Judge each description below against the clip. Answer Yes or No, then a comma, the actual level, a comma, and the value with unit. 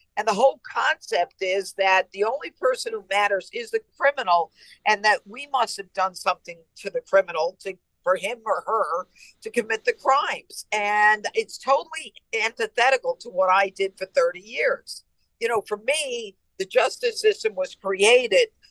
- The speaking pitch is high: Yes, high, 240 Hz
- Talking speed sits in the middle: Yes, average, 170 wpm